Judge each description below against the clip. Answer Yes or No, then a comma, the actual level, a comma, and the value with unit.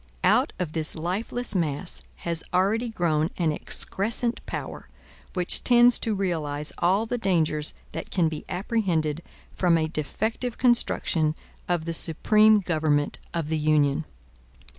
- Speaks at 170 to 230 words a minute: No, slow, 135 wpm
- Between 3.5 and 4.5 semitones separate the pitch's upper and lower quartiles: No, average, 5.3 semitones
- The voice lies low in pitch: No, medium, 170 Hz